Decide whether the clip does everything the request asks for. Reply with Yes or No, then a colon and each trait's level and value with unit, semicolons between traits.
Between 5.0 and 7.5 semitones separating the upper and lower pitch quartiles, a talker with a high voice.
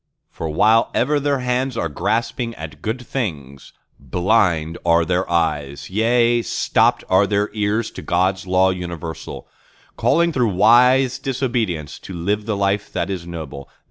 No: wide, 5.6 semitones; low, 100 Hz